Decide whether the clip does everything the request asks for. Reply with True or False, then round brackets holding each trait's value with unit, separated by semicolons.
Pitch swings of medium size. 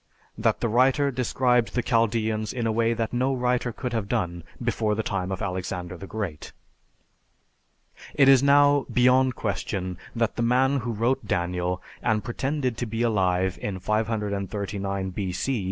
True (4.2 semitones)